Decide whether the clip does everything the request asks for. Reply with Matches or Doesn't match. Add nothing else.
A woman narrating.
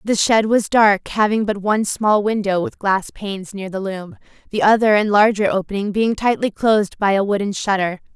Matches